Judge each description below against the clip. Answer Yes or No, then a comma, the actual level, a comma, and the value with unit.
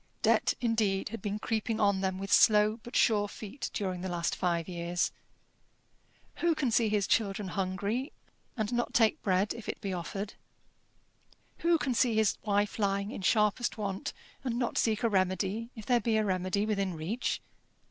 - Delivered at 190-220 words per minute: No, average, 175 wpm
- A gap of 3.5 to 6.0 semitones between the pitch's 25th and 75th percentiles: No, average, 2.9 semitones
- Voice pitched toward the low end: No, high, 210 Hz